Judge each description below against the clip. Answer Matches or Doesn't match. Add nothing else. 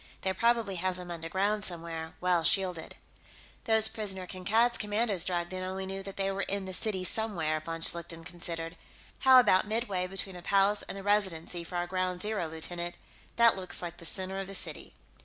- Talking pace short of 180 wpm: Doesn't match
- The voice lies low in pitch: Doesn't match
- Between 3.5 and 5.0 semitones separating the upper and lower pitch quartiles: Doesn't match